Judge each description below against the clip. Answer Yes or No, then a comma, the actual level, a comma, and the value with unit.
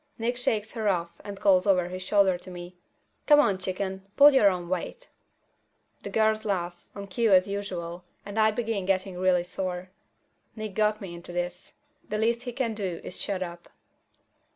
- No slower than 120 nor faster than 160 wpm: No, average, 180 wpm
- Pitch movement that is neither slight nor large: Yes, average, 3.2 semitones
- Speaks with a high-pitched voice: Yes, high, 195 Hz